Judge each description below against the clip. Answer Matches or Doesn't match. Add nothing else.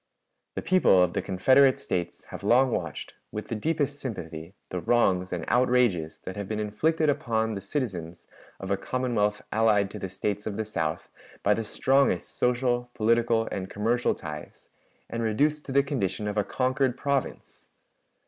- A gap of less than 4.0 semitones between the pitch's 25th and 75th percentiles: Doesn't match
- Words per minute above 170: Doesn't match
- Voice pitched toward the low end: Matches